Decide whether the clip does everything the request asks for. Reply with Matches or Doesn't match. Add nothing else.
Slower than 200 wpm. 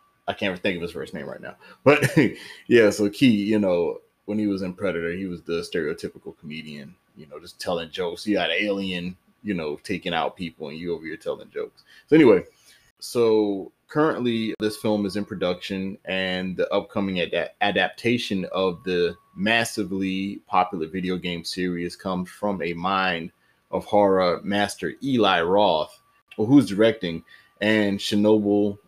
Matches